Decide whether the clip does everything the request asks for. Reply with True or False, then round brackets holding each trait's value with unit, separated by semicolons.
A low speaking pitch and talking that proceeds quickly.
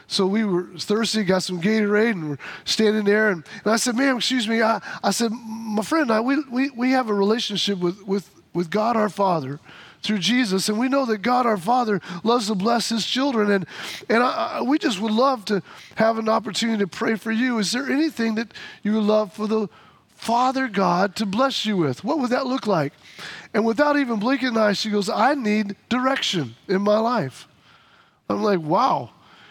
False (220 Hz; 210 wpm)